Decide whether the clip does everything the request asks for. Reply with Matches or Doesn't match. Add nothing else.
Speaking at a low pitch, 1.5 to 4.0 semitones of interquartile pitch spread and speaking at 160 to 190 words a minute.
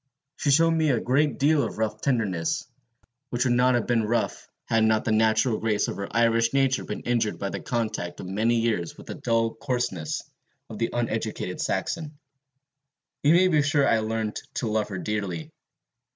Matches